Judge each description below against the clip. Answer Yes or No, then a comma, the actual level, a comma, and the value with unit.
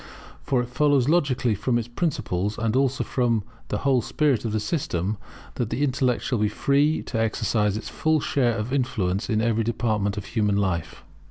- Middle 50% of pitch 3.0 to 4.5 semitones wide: Yes, average, 4.0 semitones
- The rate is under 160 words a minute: No, average, 185 wpm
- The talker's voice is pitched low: Yes, low, 120 Hz